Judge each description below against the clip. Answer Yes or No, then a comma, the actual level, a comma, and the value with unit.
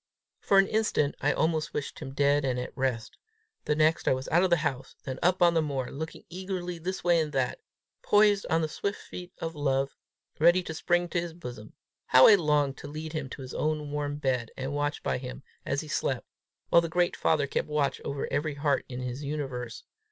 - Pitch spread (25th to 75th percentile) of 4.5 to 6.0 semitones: No, average, 3.8 semitones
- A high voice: No, medium, 150 Hz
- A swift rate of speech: Yes, fast, 220 wpm